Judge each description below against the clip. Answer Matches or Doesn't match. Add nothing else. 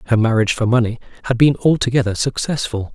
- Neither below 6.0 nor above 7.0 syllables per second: Matches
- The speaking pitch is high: Doesn't match